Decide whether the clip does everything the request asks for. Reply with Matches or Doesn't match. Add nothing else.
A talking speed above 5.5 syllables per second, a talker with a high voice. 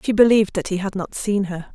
Matches